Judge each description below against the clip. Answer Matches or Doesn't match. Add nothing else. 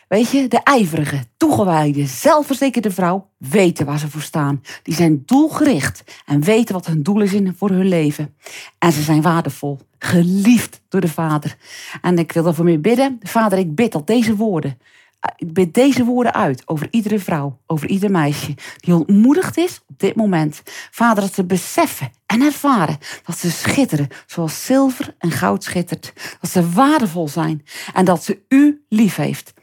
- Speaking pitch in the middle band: Matches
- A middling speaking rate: Matches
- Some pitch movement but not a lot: Doesn't match